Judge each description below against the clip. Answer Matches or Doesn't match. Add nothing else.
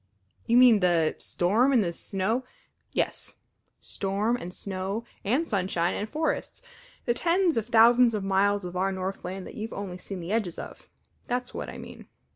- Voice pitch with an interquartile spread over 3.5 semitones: Matches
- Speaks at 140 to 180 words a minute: Matches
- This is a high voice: Matches